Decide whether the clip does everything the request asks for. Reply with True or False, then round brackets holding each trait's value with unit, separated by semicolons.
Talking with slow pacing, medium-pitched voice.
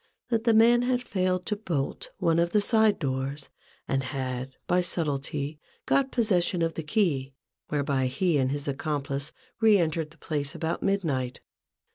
False (160 wpm; 160 Hz)